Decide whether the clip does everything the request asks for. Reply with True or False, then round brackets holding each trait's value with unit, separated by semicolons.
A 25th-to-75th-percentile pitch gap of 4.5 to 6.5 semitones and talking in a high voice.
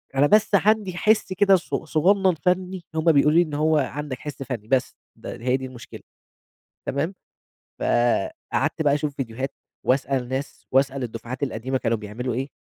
False (5.0 semitones; 140 Hz)